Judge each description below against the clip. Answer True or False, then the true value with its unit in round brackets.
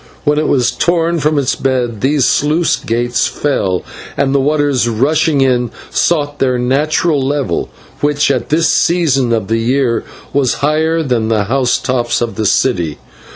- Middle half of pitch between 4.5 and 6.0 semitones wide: False (3.6 semitones)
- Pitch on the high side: False (135 Hz)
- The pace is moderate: True (160 wpm)